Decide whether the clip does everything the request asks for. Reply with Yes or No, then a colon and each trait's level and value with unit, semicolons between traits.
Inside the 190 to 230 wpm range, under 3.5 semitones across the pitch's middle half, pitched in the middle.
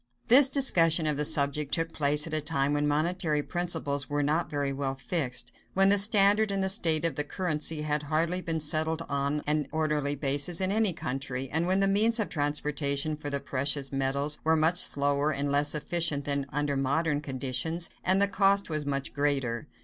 Yes: average, 195 wpm; average, 3.0 semitones; medium, 150 Hz